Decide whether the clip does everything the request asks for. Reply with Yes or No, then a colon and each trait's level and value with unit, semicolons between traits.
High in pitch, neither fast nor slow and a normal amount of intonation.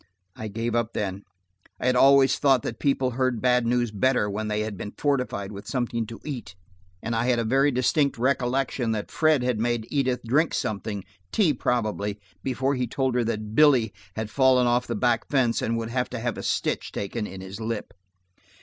No: low, 120 Hz; average, 195 wpm; average, 3.1 semitones